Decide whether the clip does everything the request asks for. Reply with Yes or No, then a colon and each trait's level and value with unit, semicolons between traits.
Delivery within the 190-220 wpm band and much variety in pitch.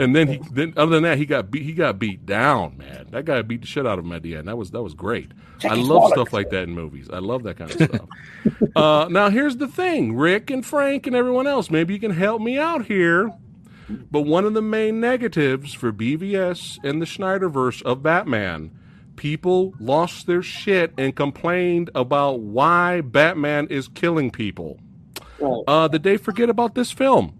Yes: fast, 205 wpm; wide, 8.0 semitones